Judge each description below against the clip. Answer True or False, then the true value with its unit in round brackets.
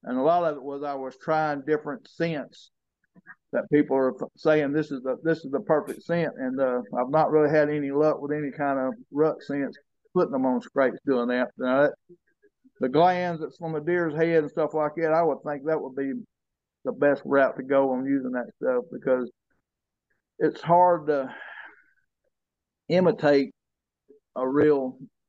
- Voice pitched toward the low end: False (150 Hz)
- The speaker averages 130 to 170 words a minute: False (185 wpm)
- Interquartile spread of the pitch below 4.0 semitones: True (3.4 semitones)